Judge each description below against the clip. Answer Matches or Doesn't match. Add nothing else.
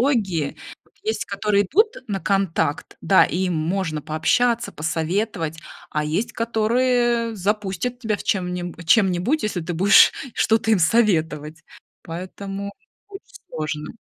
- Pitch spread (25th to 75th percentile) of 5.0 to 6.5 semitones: Matches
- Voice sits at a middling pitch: Doesn't match